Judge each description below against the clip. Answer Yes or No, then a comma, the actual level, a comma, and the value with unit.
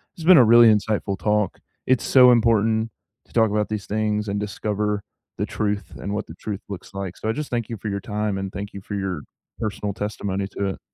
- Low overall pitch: Yes, low, 105 Hz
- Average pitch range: No, narrow, 1.8 semitones